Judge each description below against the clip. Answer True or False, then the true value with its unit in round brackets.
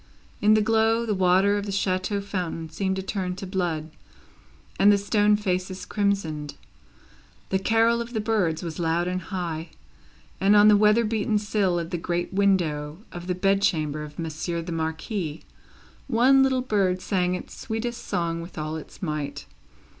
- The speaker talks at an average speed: True (170 wpm)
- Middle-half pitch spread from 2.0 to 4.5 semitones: True (3.9 semitones)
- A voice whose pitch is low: False (190 Hz)